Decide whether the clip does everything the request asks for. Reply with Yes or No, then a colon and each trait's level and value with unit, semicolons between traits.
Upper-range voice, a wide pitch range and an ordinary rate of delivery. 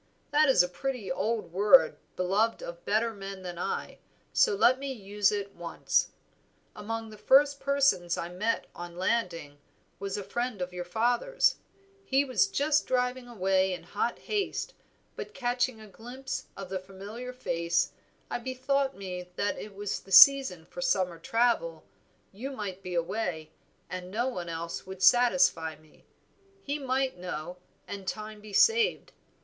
Yes: high, 210 Hz; wide, 5.9 semitones; average, 155 wpm